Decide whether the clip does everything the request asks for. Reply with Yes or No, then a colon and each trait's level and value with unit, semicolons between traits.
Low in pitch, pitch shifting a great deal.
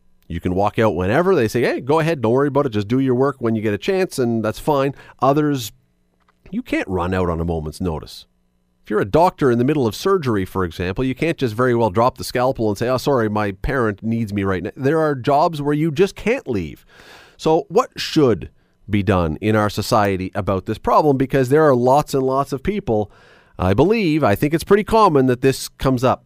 Yes: low, 120 Hz; wide, 5.8 semitones